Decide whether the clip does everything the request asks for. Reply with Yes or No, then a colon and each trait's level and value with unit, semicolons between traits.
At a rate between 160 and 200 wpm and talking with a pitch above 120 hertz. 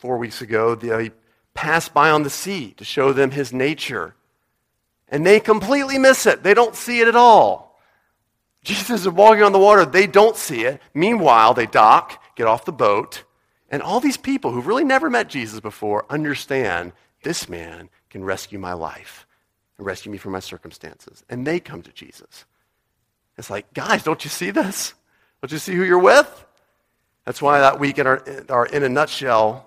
Yes: average, 190 wpm; medium, 140 Hz